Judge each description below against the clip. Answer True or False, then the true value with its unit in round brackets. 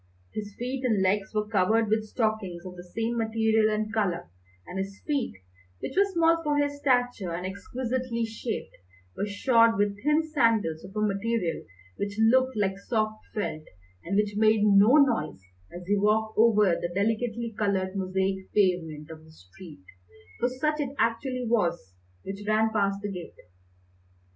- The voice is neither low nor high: False (215 Hz)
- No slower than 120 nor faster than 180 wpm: True (165 wpm)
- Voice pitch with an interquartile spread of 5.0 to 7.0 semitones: False (3.4 semitones)